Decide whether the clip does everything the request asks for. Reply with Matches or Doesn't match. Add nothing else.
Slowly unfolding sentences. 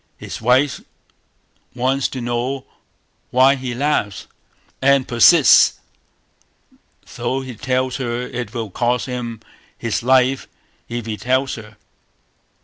Matches